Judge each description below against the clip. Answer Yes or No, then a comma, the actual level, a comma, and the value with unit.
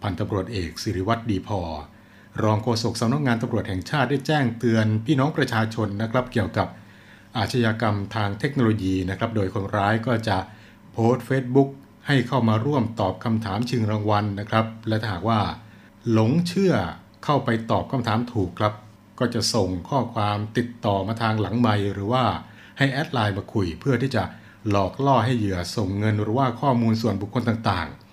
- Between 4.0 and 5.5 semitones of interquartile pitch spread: No, average, 2.8 semitones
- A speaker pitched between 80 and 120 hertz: Yes, low, 110 Hz